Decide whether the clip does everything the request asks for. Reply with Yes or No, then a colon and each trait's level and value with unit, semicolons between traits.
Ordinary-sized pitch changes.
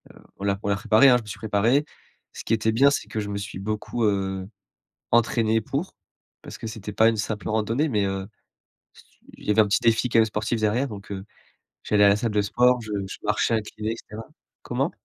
No: narrow, 1.9 semitones